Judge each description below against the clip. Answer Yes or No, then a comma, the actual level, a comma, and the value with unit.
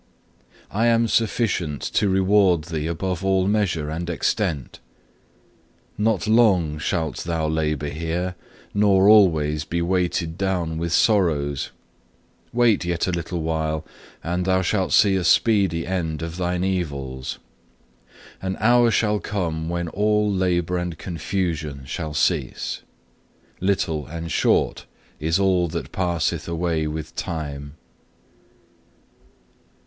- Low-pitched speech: Yes, very low, 85 Hz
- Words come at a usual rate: No, slow, 120 wpm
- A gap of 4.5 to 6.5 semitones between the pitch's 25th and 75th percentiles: No, average, 3.3 semitones